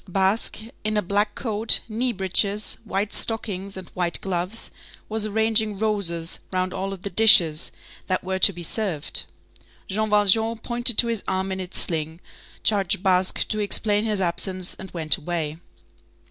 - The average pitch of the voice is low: No, high, 195 Hz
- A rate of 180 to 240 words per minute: No, average, 160 wpm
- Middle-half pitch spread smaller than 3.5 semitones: Yes, average, 2.9 semitones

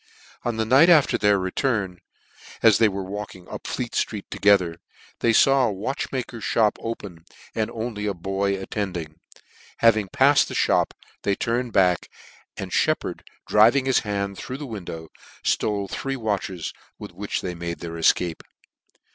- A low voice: Yes, low, 105 Hz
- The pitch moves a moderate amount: Yes, average, 3.7 semitones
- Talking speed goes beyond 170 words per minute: No, average, 160 wpm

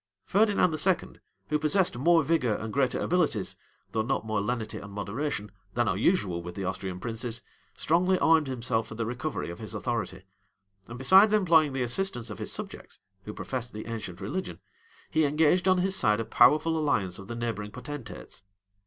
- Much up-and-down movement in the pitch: Yes, wide, 6.8 semitones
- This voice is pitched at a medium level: No, low, 120 Hz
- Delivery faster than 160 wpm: Yes, average, 185 wpm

